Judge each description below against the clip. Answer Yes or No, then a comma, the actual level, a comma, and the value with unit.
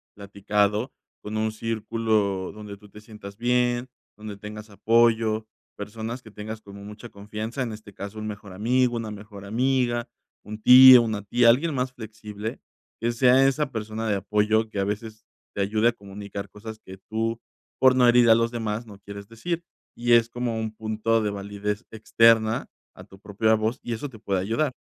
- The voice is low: Yes, low, 110 Hz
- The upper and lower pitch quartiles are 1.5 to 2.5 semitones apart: Yes, narrow, 2.1 semitones